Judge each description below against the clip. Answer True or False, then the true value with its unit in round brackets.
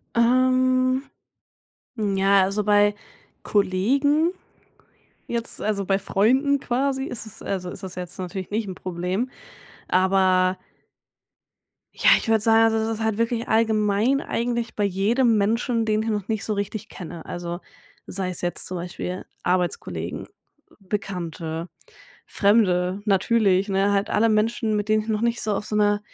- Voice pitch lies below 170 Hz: False (210 Hz)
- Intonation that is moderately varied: True (3.3 semitones)